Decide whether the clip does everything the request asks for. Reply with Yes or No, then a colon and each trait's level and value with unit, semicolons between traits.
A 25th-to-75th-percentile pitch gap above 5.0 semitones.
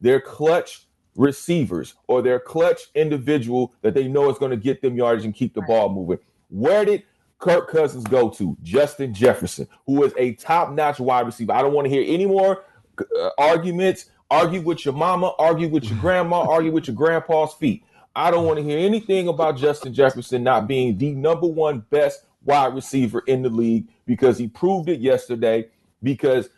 Yes: wide, 5.4 semitones